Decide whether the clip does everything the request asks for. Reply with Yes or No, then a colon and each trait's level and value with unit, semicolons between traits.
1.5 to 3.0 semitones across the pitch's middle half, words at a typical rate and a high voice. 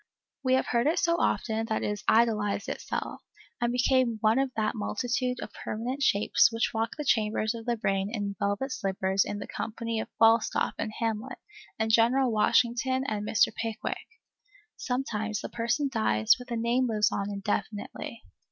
Yes: average, 2.7 semitones; average, 170 wpm; high, 225 Hz